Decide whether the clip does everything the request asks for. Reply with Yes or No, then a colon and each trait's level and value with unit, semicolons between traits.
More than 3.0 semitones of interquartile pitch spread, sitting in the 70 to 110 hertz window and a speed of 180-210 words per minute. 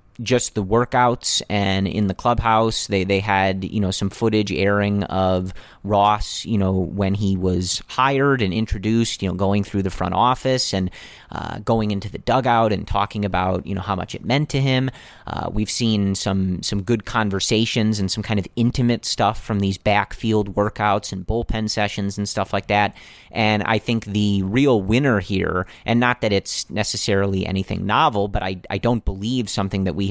No: narrow, 2.6 semitones; low, 105 Hz; average, 190 wpm